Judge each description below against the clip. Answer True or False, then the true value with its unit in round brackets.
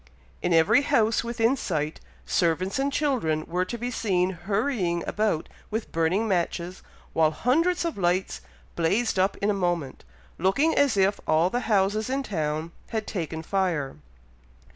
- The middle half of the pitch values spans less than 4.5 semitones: False (5.3 semitones)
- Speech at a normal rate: True (150 wpm)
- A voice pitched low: False (190 Hz)